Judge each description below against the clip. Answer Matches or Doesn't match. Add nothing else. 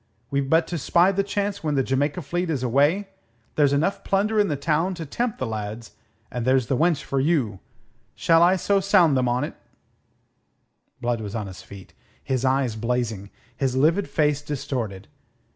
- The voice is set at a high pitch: Doesn't match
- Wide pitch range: Matches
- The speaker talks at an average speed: Matches